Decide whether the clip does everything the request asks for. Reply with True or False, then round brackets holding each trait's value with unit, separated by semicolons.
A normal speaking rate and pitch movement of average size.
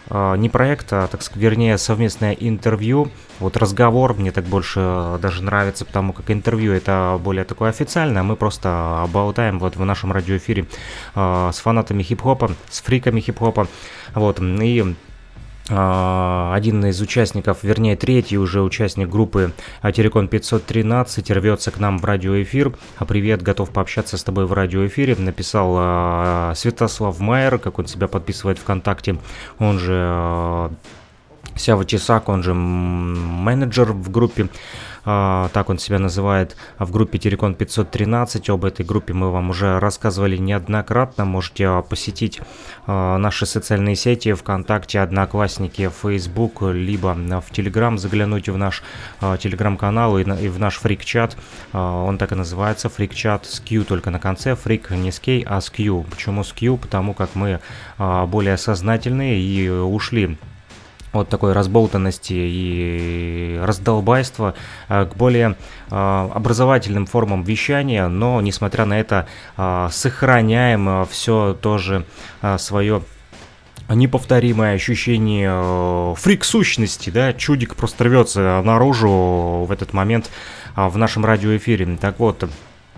True (125 wpm; 3.0 semitones)